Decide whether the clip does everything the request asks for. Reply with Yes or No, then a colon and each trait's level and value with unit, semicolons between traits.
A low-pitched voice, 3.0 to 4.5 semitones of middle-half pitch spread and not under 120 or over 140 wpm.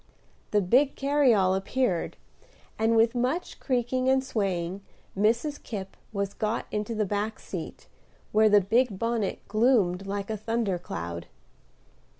No: high, 215 Hz; average, 3.8 semitones; slow, 135 wpm